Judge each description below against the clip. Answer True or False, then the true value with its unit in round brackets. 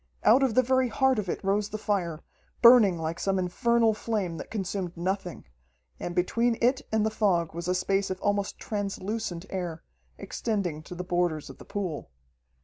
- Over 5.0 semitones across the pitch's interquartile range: False (3.9 semitones)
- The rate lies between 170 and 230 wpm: True (180 wpm)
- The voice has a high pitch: True (195 Hz)